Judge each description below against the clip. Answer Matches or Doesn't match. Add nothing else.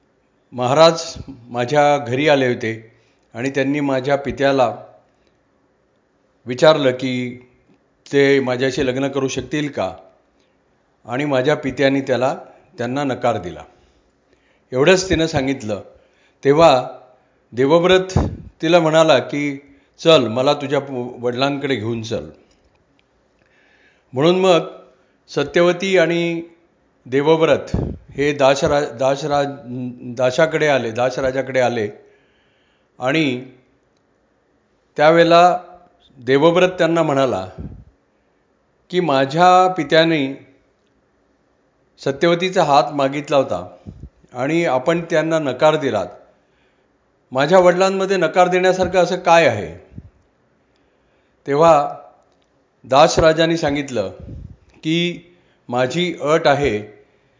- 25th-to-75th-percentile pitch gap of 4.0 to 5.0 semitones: Matches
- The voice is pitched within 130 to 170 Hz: Matches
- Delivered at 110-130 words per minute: Doesn't match